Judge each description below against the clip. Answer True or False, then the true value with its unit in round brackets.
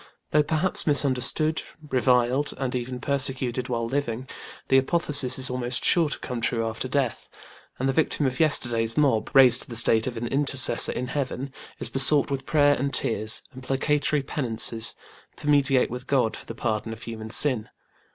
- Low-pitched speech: True (130 Hz)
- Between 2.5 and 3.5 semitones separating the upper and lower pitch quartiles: True (3.0 semitones)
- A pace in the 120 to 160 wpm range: False (170 wpm)